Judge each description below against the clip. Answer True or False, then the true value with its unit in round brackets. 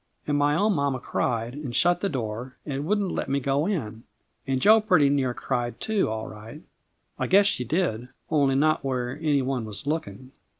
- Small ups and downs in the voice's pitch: False (4.5 semitones)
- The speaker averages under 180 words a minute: False (195 wpm)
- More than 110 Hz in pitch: True (140 Hz)